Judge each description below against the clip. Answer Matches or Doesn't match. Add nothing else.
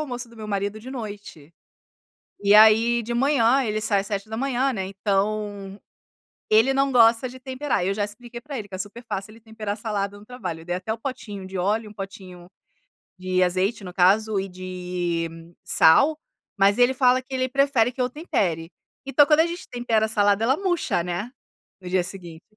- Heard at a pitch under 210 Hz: Doesn't match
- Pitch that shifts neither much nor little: Matches